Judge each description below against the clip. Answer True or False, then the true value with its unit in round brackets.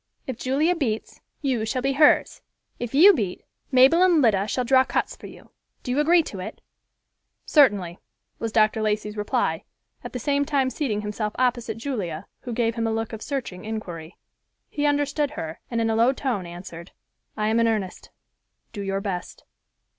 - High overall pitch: True (230 Hz)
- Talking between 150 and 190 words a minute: True (180 wpm)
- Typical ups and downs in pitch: True (4.6 semitones)